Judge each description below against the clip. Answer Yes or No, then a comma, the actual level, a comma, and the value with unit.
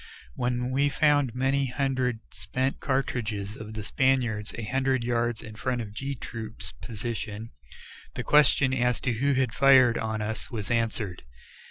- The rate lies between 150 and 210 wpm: Yes, average, 155 wpm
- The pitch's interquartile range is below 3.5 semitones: Yes, average, 3.1 semitones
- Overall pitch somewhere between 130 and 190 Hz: No, low, 120 Hz